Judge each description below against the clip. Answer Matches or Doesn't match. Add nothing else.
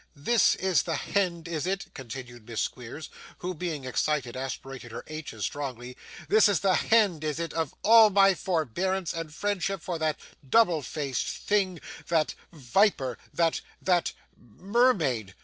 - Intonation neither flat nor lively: Doesn't match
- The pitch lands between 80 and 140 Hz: Doesn't match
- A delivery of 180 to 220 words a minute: Doesn't match